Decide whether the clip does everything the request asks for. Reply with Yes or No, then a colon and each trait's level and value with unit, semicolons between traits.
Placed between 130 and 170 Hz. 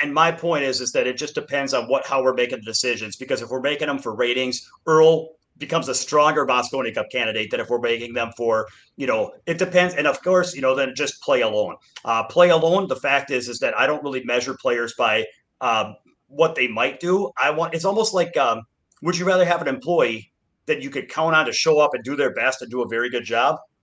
Yes: medium, 140 Hz